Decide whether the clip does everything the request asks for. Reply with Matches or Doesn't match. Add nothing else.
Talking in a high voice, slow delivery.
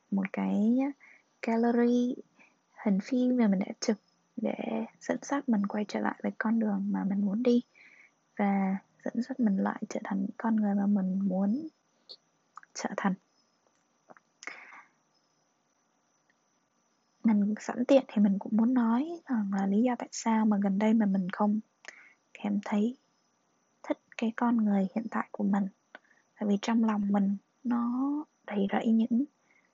Matches